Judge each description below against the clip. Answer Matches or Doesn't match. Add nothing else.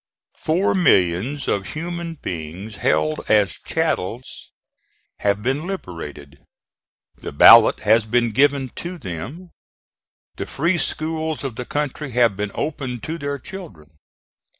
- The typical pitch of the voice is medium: Doesn't match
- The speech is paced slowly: Matches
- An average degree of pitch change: Doesn't match